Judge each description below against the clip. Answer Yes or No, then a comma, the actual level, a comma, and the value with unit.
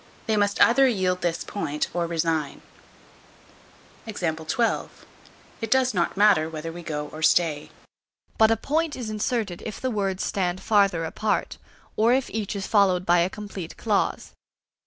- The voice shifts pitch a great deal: No, average, 4.5 semitones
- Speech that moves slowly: No, average, 150 wpm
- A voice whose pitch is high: Yes, high, 195 Hz